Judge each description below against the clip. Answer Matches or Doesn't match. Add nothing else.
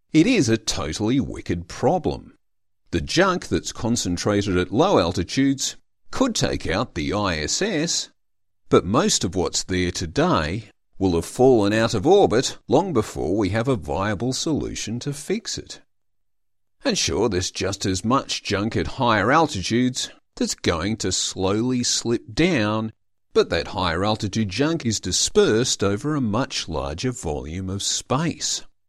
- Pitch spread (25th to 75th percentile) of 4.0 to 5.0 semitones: Matches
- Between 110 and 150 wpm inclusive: Matches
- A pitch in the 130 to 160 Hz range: Doesn't match